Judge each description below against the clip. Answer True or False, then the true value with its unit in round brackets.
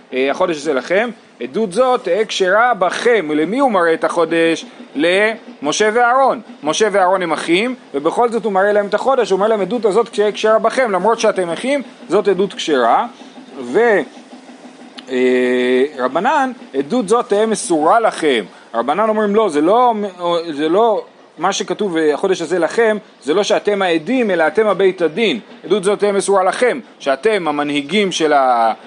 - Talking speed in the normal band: False (155 wpm)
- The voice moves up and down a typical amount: False (6.0 semitones)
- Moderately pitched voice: False (210 Hz)